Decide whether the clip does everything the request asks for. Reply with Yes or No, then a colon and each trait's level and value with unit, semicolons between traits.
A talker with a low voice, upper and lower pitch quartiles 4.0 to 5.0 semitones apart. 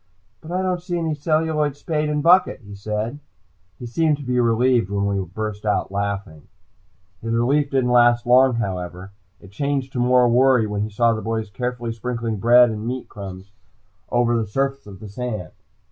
Yes: low, 120 Hz; average, 4.5 semitones